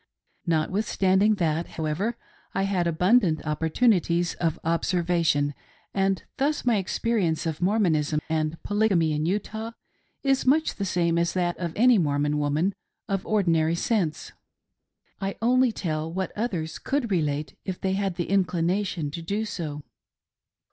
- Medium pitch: Yes, medium, 180 Hz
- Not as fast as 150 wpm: Yes, slow, 135 wpm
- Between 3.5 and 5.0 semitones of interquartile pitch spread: Yes, average, 4.2 semitones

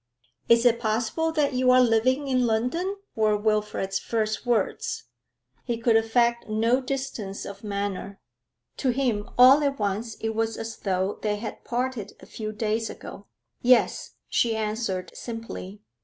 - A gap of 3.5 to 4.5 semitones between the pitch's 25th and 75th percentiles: No, average, 2.9 semitones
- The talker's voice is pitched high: Yes, high, 225 Hz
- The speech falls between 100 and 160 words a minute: Yes, average, 150 wpm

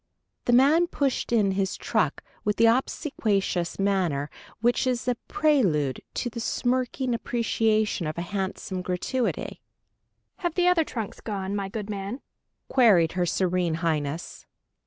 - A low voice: No, high, 210 Hz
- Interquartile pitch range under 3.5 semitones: No, average, 5.3 semitones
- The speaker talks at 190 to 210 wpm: No, slow, 135 wpm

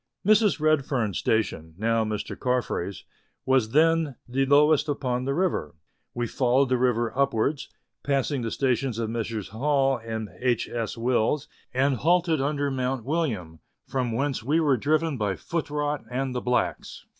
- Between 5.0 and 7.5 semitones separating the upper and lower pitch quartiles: No, average, 4.2 semitones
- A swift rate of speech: No, average, 155 wpm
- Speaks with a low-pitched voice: Yes, low, 130 Hz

